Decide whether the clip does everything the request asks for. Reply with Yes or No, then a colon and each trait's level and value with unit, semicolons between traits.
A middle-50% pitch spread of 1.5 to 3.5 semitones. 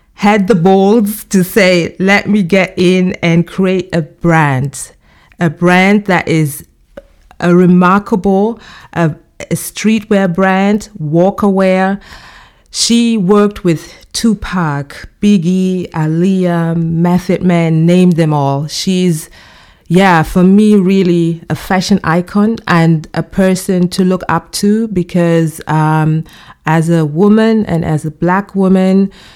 Yes: average, 3.0 semitones